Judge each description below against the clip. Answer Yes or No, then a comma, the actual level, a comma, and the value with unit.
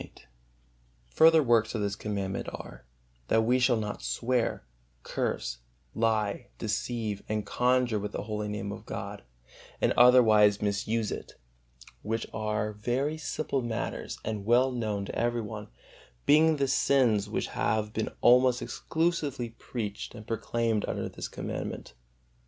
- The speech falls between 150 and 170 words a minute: No, average, 140 wpm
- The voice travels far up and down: No, average, 2.9 semitones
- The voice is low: Yes, low, 115 Hz